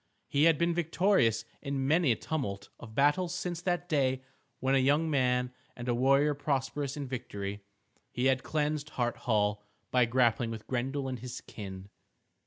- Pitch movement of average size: Yes, average, 3.8 semitones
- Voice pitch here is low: Yes, low, 130 Hz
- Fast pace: No, average, 170 wpm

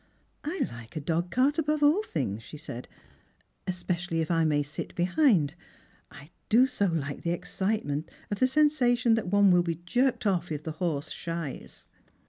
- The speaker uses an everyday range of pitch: No, wide, 7.6 semitones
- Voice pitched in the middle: Yes, medium, 175 Hz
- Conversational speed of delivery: Yes, average, 175 wpm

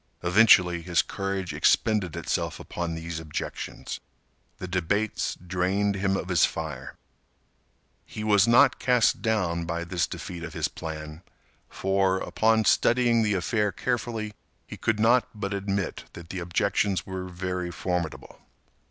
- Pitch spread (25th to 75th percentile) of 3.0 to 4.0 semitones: Yes, average, 3.5 semitones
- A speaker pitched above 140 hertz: No, very low, 95 Hz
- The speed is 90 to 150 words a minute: Yes, slow, 135 wpm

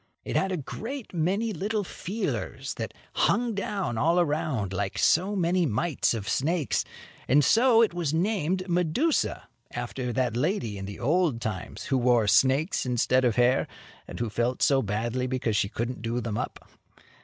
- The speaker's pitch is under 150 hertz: Yes, medium, 140 Hz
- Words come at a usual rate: Yes, average, 165 wpm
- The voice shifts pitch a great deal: Yes, wide, 7.5 semitones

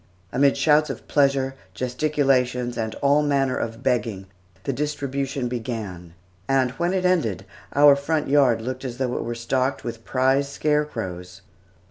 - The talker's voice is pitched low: Yes, low, 130 Hz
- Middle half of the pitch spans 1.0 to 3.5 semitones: Yes, average, 3.2 semitones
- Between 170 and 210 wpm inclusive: No, average, 145 wpm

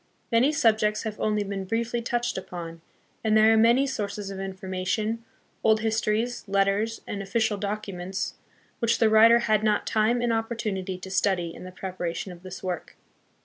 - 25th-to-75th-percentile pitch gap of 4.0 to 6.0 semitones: No, average, 3.0 semitones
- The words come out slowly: No, average, 165 wpm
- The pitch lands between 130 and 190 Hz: No, high, 215 Hz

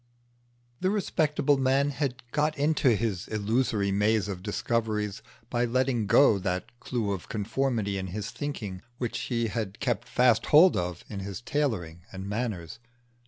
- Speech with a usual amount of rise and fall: Yes, average, 4.9 semitones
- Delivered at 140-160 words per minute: Yes, average, 150 wpm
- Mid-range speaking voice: No, low, 115 Hz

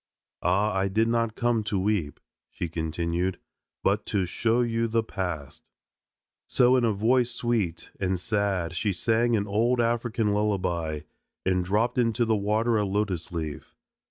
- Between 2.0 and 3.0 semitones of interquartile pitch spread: No, average, 4.0 semitones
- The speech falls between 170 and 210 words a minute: No, average, 155 wpm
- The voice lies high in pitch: No, low, 105 Hz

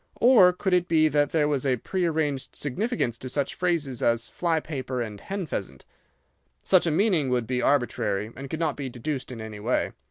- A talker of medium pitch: Yes, medium, 145 Hz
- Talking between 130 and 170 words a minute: No, average, 195 wpm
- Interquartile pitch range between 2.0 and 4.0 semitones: No, average, 5.2 semitones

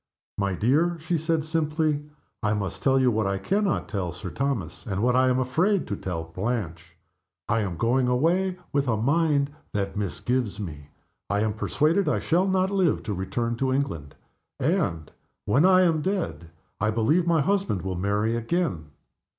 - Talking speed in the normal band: Yes, average, 175 wpm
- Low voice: Yes, low, 125 Hz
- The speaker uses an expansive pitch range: Yes, wide, 8.3 semitones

